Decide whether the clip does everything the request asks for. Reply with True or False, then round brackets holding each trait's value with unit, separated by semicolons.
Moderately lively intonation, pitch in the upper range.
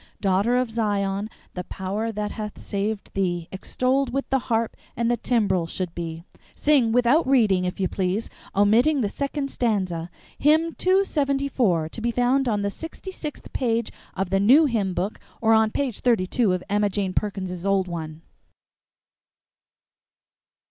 True (4.8 semitones; 215 Hz)